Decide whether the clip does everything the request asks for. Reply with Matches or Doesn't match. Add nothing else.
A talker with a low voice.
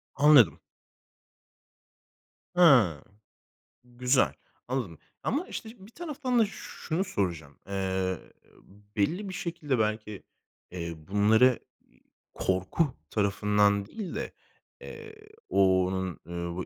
Matches